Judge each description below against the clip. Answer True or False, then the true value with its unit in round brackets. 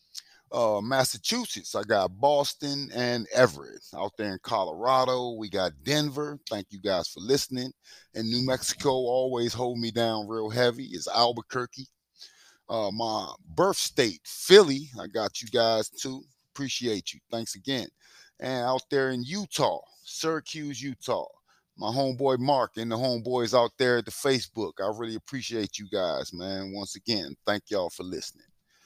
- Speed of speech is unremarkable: True (155 wpm)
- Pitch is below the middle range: True (125 Hz)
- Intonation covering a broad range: False (3.3 semitones)